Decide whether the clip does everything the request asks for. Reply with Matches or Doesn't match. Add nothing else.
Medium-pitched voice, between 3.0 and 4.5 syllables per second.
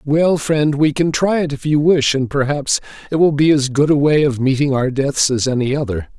Doesn't match